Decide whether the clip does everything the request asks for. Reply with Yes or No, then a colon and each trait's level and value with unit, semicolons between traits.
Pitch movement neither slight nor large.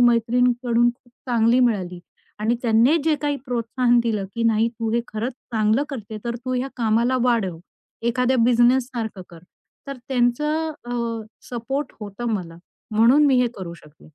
No: narrow, 2.3 semitones